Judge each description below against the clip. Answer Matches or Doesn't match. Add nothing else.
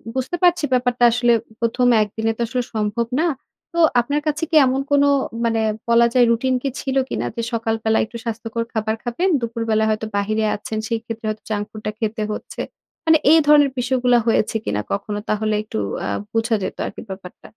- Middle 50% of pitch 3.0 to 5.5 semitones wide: Doesn't match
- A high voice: Matches